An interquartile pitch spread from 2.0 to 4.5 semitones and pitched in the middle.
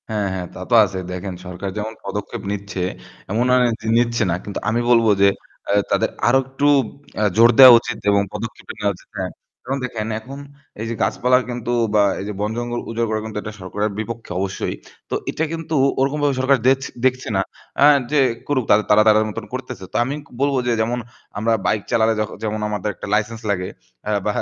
No: average, 3.3 semitones; low, 110 Hz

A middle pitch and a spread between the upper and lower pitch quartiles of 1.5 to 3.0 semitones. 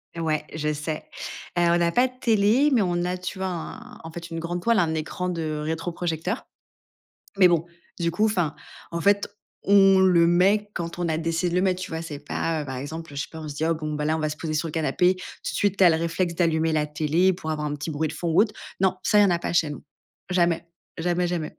Yes: medium, 170 Hz; narrow, 2.5 semitones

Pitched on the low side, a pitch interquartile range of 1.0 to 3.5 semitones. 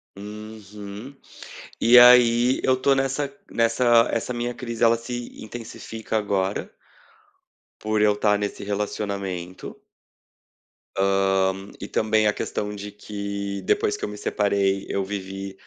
Yes: low, 105 Hz; average, 2.7 semitones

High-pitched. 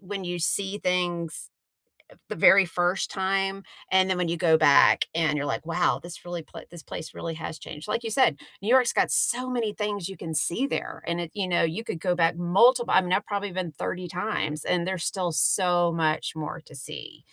No: medium, 180 Hz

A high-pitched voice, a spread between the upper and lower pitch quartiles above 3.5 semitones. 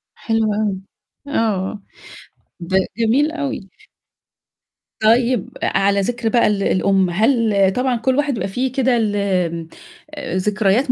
Yes: high, 220 Hz; average, 4.1 semitones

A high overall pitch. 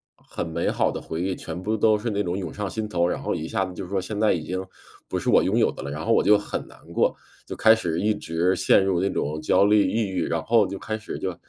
No: very low, 95 Hz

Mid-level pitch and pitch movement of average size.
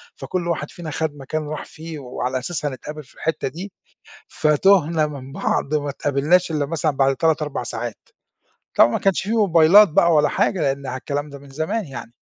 Yes: medium, 150 Hz; average, 3.1 semitones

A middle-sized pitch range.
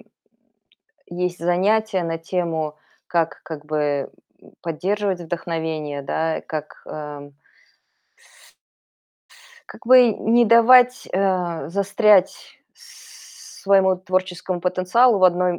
Yes: average, 3.5 semitones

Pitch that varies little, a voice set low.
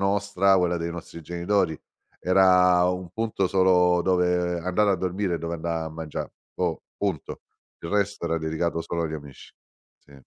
Yes: narrow, 2.1 semitones; very low, 90 Hz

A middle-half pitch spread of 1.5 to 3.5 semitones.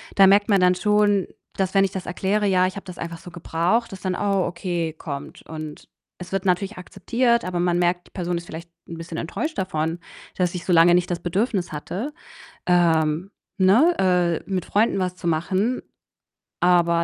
Yes: narrow, 2.4 semitones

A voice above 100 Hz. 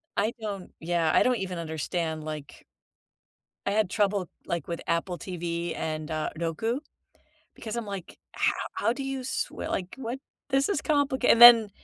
Yes: high, 190 Hz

